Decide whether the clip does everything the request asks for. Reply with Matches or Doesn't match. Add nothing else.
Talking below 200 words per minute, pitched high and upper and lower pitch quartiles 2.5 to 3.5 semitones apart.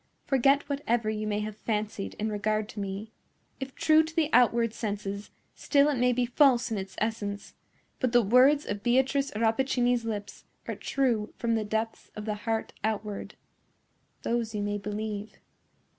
Matches